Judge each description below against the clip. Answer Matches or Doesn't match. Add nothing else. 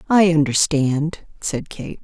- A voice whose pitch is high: Doesn't match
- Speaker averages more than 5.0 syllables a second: Doesn't match